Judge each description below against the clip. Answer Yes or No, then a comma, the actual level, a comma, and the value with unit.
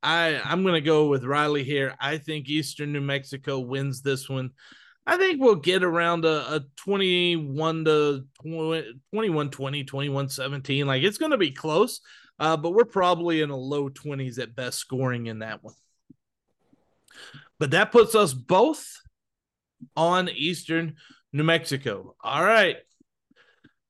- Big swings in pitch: No, average, 3.6 semitones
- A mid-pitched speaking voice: Yes, medium, 150 Hz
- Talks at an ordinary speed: Yes, average, 155 wpm